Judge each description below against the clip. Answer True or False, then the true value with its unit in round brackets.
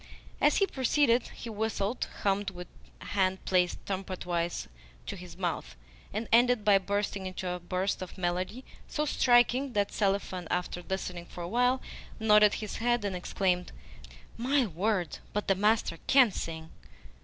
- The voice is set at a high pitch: True (200 Hz)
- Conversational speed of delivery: True (150 wpm)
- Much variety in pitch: False (4.1 semitones)